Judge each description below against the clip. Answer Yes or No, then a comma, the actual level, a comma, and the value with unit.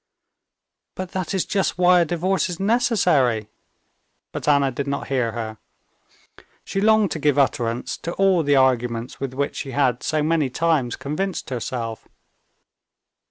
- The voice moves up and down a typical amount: No, wide, 6.1 semitones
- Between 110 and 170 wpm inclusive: Yes, average, 150 wpm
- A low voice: No, medium, 145 Hz